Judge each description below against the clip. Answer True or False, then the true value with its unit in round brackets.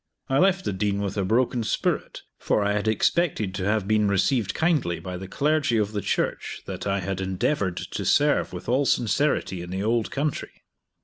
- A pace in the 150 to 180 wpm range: False (195 wpm)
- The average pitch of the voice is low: True (105 Hz)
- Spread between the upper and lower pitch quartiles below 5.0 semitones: False (5.3 semitones)